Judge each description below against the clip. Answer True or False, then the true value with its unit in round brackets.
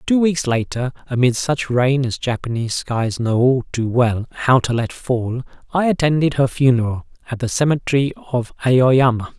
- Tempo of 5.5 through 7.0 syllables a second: False (4.9 syllables/s)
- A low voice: True (125 Hz)